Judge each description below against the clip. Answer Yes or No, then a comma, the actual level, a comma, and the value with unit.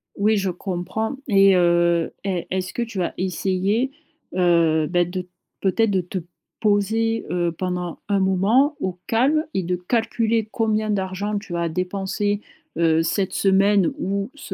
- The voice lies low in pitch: No, high, 190 Hz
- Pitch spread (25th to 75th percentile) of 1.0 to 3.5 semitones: Yes, average, 3.1 semitones